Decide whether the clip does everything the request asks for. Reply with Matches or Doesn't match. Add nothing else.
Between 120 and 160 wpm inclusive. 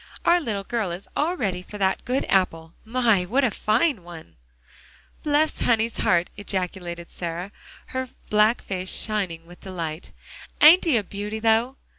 Matches